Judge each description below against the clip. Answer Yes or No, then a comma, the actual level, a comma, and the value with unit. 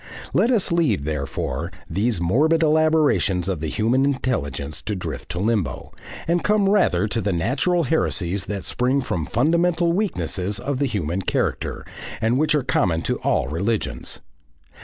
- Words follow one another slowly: No, average, 155 wpm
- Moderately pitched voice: No, low, 115 Hz